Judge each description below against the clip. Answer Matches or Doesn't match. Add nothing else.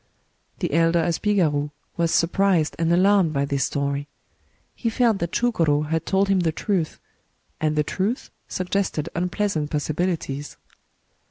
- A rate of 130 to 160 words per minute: Matches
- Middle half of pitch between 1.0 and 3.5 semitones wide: Doesn't match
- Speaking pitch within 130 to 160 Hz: Doesn't match